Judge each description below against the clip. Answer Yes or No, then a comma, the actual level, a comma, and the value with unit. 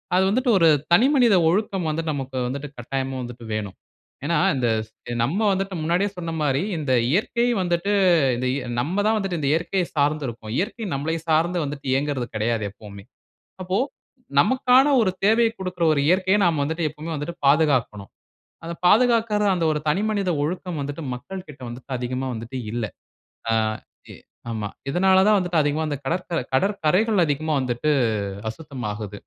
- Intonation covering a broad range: Yes, wide, 6.1 semitones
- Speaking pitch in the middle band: Yes, medium, 160 Hz